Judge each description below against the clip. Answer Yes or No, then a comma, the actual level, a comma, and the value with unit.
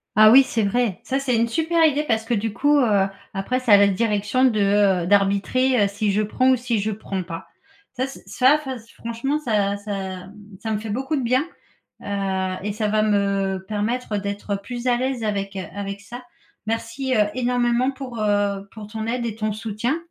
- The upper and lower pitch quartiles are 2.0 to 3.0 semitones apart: No, average, 3.7 semitones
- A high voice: Yes, high, 220 Hz